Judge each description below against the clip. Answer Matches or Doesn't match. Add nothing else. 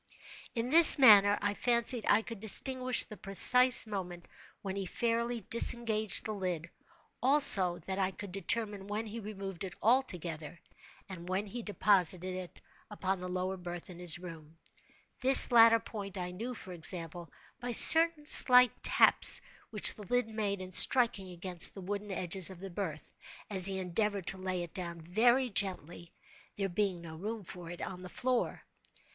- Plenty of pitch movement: Doesn't match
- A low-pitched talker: Doesn't match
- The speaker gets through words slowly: Doesn't match